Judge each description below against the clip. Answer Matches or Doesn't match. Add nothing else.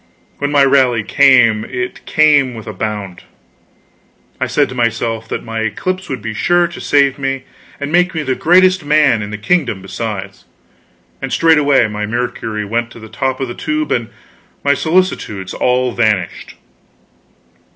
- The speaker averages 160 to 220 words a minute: Matches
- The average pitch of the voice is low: Matches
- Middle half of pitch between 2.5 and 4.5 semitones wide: Doesn't match